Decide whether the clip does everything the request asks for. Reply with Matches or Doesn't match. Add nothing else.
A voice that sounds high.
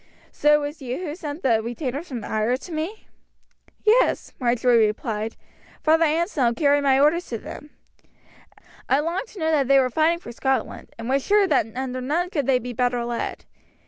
Matches